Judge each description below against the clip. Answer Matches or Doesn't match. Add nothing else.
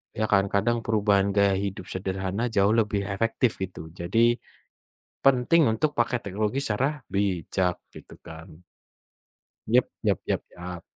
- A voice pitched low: Matches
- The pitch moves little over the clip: Doesn't match